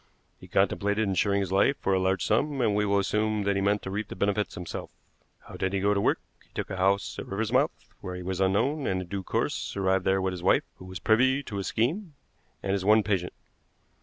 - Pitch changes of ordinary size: No, narrow, 2.2 semitones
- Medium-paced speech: No, fast, 240 wpm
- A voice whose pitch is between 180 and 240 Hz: No, low, 100 Hz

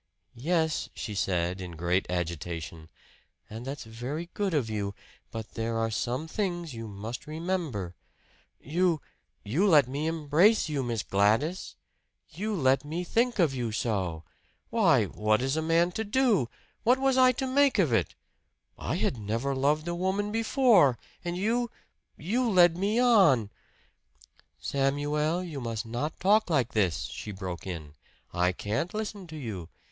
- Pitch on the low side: No, medium, 145 Hz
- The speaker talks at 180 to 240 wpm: No, average, 160 wpm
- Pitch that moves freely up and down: Yes, wide, 8.8 semitones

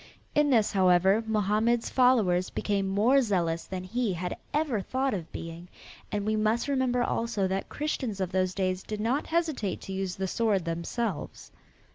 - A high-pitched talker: Yes, high, 205 Hz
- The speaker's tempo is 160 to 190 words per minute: Yes, average, 165 wpm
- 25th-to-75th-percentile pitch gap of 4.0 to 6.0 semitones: Yes, average, 4.4 semitones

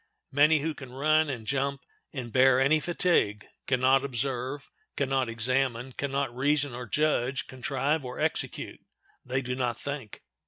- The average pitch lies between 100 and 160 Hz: Yes, low, 135 Hz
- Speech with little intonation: Yes, narrow, 2.3 semitones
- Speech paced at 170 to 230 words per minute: No, average, 155 wpm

